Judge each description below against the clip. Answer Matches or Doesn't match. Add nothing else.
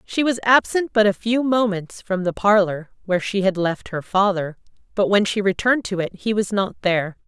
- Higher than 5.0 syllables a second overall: Matches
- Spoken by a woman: Matches